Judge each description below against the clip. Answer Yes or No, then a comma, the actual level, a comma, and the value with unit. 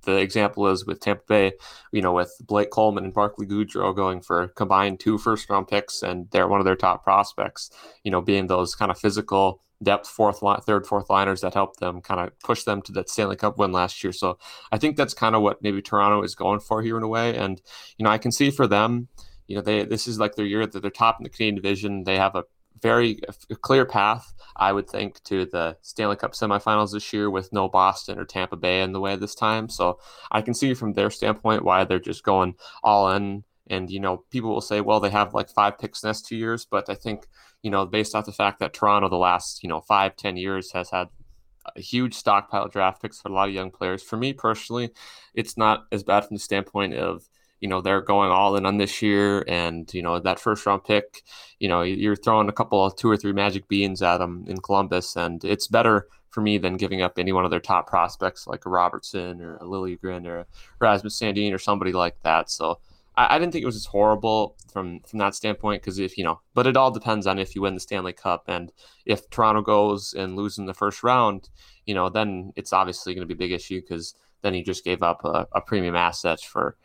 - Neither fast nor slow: No, fast, 245 wpm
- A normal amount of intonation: No, narrow, 2.3 semitones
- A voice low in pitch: Yes, low, 100 Hz